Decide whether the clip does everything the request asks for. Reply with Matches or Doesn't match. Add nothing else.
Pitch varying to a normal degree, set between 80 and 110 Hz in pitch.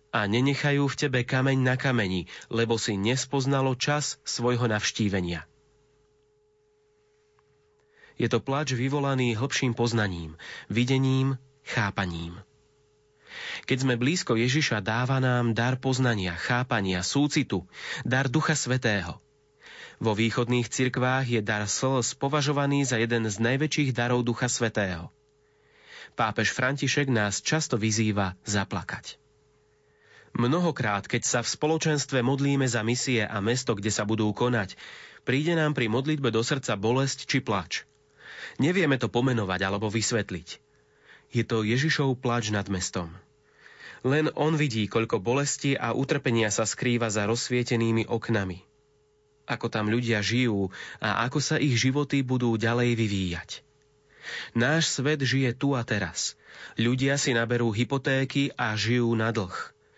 Doesn't match